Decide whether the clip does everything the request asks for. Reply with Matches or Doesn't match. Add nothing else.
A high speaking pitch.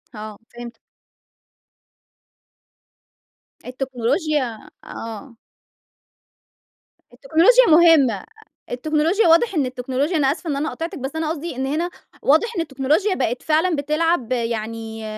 Matches